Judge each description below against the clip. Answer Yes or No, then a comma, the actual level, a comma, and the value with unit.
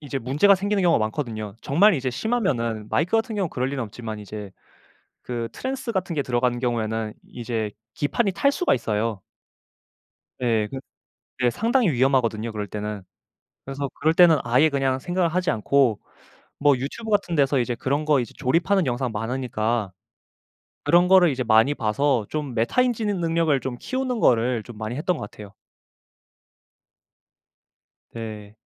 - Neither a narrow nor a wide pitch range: No, wide, 6.9 semitones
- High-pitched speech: No, low, 130 Hz